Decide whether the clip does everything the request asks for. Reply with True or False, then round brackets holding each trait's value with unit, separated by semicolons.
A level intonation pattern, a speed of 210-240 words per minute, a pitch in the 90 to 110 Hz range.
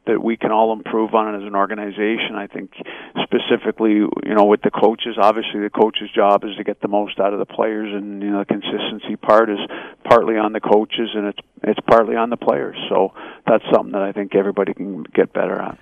True (1.5 semitones; 225 wpm; 105 Hz)